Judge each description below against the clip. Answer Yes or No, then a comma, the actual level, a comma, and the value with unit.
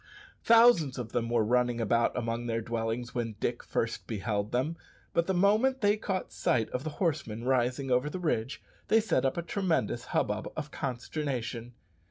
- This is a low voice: Yes, low, 125 Hz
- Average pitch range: No, wide, 6.0 semitones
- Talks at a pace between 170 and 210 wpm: Yes, average, 175 wpm